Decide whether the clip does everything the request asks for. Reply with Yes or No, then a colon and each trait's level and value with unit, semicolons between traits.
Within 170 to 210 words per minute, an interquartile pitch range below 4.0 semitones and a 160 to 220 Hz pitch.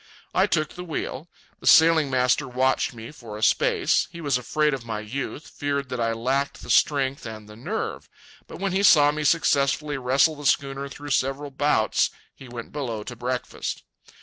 No: average, 185 wpm; average, 3.0 semitones; low, 135 Hz